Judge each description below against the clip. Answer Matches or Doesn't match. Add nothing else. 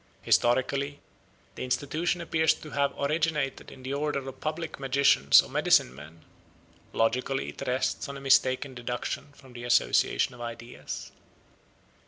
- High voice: Doesn't match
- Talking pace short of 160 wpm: Matches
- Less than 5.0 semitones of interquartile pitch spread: Matches